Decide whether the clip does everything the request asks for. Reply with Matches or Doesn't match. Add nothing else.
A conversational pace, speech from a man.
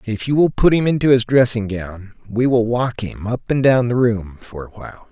Doesn't match